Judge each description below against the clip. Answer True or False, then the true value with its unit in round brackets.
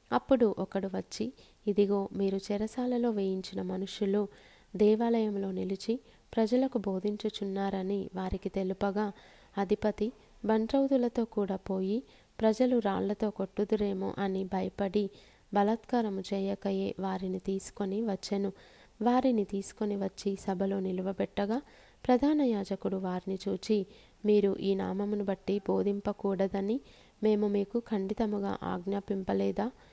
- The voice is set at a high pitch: True (200 Hz)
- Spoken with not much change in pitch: True (1.8 semitones)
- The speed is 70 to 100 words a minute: True (90 wpm)